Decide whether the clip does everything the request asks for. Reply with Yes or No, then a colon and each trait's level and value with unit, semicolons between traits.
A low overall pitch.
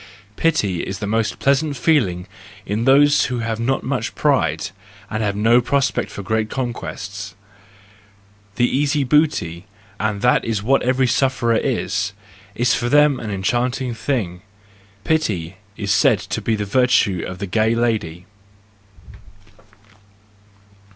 Yes: low, 115 Hz